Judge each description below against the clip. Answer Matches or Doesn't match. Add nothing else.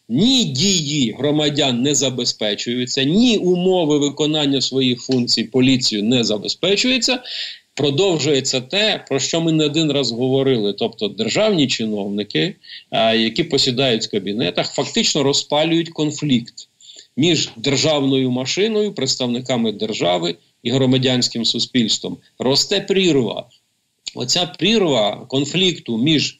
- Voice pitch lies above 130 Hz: Matches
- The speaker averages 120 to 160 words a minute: Doesn't match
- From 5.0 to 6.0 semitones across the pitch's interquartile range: Matches